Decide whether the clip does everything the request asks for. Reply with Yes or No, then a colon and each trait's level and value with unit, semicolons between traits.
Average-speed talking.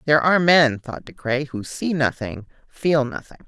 Yes: average, 190 wpm